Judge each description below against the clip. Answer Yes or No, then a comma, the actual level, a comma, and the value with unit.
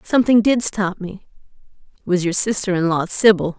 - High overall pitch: Yes, high, 195 Hz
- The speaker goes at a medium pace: Yes, average, 185 wpm